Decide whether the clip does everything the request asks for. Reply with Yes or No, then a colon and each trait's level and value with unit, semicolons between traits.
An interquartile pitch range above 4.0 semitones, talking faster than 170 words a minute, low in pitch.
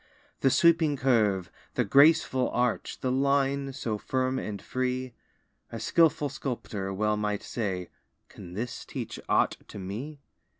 No: average, 4.7 semitones; slow, 135 wpm; low, 125 Hz